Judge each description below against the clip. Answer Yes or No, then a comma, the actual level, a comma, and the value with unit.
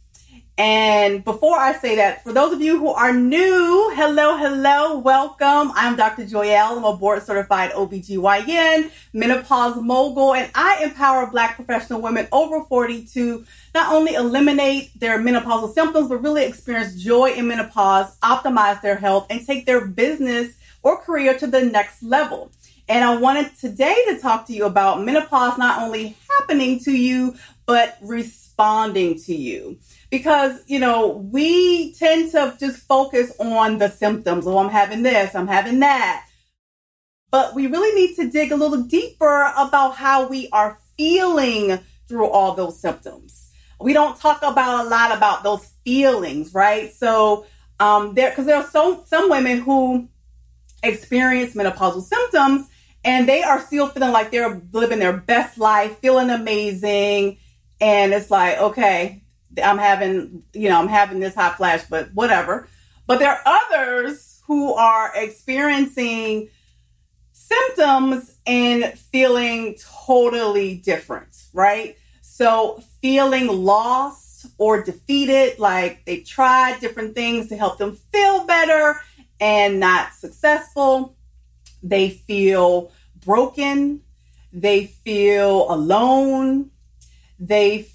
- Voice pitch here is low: No, high, 240 Hz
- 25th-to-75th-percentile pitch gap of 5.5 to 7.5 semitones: No, average, 5.1 semitones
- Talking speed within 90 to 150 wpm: Yes, average, 140 wpm